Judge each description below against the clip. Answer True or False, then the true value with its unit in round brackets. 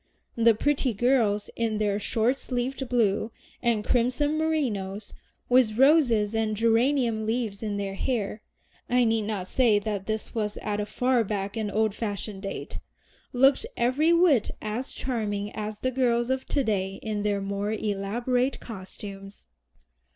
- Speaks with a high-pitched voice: True (220 Hz)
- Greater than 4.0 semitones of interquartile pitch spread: False (3.4 semitones)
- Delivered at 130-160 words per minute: True (150 wpm)